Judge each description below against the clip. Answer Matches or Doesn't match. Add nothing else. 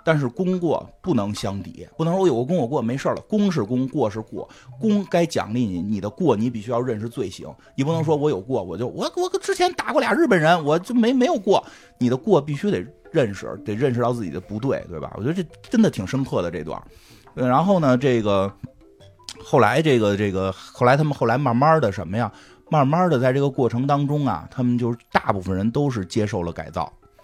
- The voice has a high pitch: Doesn't match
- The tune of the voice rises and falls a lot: Matches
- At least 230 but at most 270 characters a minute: Doesn't match